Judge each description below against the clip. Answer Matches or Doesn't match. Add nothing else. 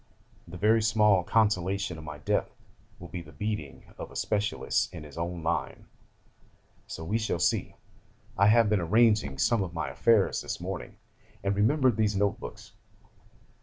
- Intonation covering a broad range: Doesn't match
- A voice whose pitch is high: Doesn't match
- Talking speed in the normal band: Matches